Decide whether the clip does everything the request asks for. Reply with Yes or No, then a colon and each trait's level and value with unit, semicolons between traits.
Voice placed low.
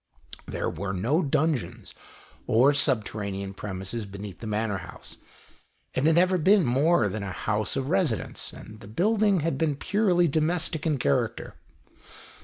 Yes: low, 130 Hz